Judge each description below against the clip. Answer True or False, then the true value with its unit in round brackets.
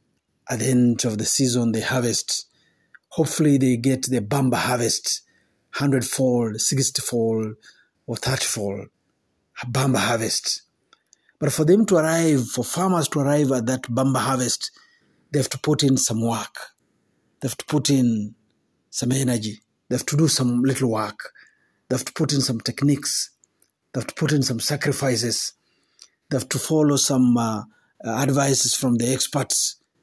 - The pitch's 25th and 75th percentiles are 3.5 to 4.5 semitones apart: False (3.1 semitones)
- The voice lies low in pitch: True (130 Hz)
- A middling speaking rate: False (165 wpm)